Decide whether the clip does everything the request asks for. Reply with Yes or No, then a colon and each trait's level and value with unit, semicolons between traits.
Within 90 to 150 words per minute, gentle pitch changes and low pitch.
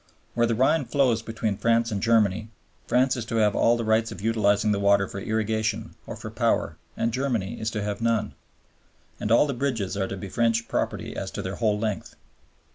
No: fast, 205 wpm; narrow, 2.1 semitones; low, 110 Hz